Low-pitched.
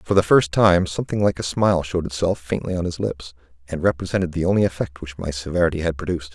Yes: very low, 85 Hz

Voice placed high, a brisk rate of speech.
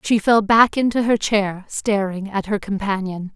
No: high, 205 Hz; average, 180 wpm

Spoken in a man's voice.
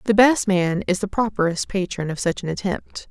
No: female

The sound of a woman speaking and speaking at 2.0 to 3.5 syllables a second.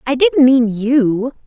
Yes: female; 3.2 syllables/s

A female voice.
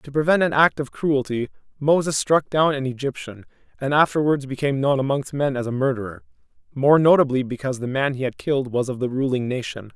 No: male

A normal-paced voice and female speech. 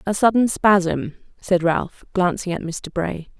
Yes: average, 160 wpm; female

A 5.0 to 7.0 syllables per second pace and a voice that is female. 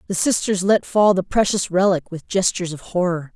Yes: 5.4 syllables/s; female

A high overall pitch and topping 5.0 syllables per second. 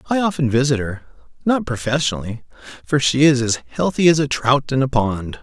No: low, 135 Hz; 5.5 syllables/s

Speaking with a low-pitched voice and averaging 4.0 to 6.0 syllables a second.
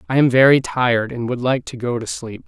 Yes: low, 125 Hz; 5.8 syllables/s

